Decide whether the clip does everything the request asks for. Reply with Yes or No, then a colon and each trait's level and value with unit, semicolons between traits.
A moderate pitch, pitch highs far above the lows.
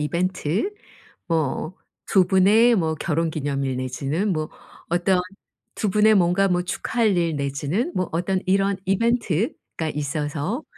No: medium, 175 Hz; average, 4.3 semitones